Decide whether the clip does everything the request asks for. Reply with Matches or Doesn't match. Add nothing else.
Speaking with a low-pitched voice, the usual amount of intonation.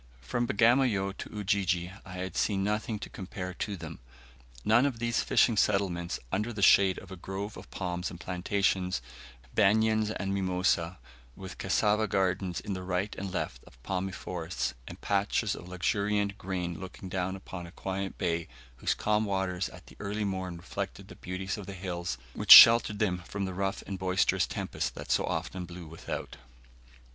Doesn't match